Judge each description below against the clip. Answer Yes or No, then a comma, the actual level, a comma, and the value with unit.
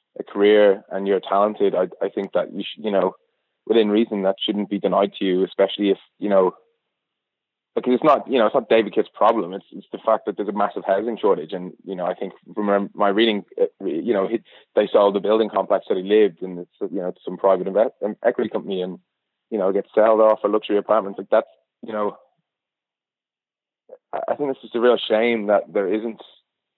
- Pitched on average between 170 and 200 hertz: No, low, 105 Hz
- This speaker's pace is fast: Yes, fast, 215 wpm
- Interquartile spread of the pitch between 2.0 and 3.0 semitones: Yes, narrow, 2.4 semitones